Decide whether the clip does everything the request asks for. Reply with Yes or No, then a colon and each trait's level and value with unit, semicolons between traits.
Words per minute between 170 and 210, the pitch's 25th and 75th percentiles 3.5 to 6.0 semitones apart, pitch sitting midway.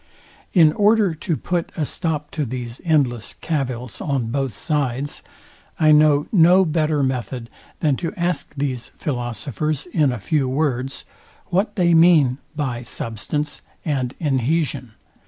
No: slow, 135 wpm; average, 4.0 semitones; medium, 145 Hz